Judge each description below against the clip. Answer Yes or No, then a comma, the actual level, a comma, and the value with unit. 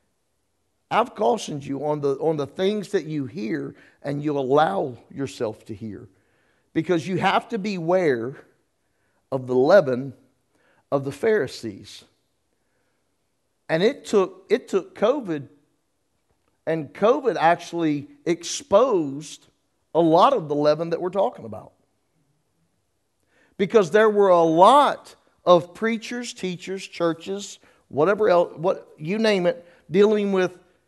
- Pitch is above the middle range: No, medium, 160 Hz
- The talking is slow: Yes, slow, 125 wpm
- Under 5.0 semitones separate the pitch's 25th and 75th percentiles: No, wide, 5.4 semitones